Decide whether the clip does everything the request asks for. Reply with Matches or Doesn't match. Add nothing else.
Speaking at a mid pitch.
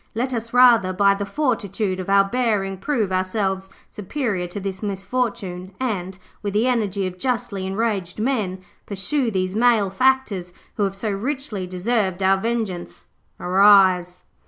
Doesn't match